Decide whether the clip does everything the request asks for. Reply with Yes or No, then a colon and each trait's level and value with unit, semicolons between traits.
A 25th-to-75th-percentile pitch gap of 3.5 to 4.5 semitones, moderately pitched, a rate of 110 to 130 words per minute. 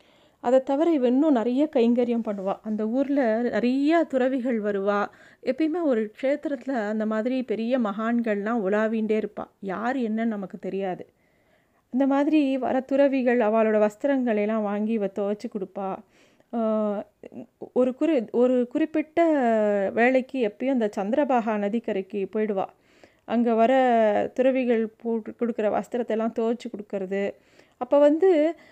No: average, 3.8 semitones; high, 235 Hz; average, 115 wpm